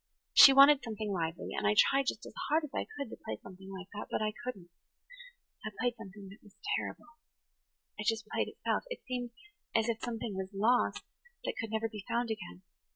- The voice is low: No, high, 220 Hz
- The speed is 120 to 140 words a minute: No, average, 195 wpm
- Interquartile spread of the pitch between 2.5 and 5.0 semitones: Yes, average, 4.0 semitones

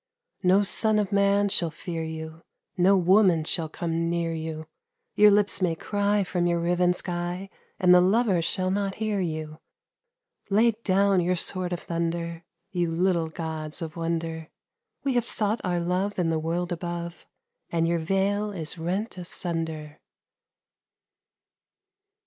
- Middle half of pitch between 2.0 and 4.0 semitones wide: Yes, average, 3.0 semitones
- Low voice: No, medium, 175 Hz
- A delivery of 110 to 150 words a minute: Yes, average, 145 wpm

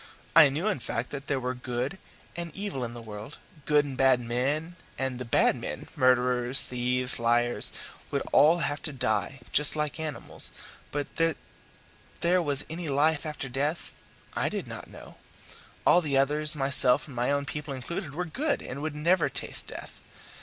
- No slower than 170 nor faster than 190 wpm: Yes, average, 180 wpm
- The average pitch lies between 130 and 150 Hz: Yes, medium, 140 Hz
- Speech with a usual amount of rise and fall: Yes, average, 3.6 semitones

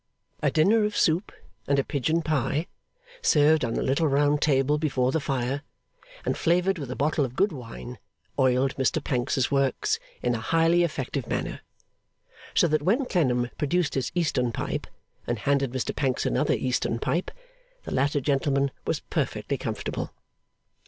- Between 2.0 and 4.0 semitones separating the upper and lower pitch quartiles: Yes, average, 3.4 semitones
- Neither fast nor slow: Yes, average, 160 wpm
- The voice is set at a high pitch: No, medium, 140 Hz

